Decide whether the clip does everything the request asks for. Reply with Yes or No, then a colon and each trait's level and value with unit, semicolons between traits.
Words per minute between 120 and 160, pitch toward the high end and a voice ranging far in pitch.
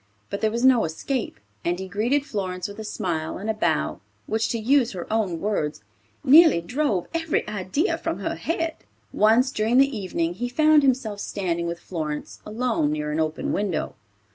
No: average, 180 wpm; high, 215 Hz; wide, 6.5 semitones